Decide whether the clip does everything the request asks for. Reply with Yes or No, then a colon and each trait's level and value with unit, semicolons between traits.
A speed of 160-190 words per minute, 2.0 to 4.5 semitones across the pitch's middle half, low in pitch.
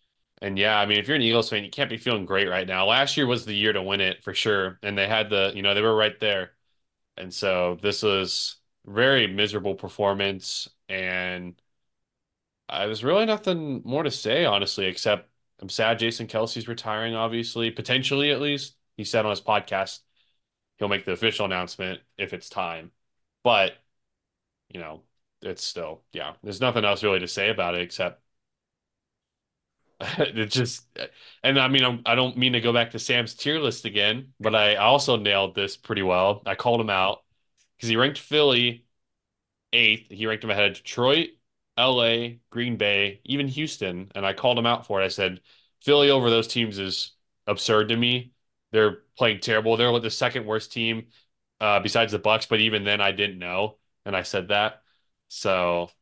Yes: average, 185 wpm; average, 3.3 semitones; low, 110 Hz